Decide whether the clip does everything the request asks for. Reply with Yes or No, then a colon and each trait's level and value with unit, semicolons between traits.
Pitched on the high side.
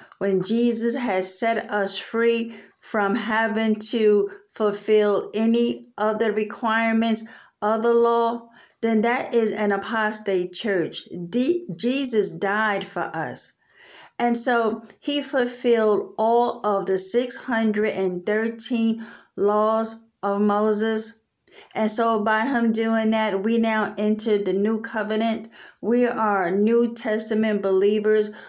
Yes: high, 220 Hz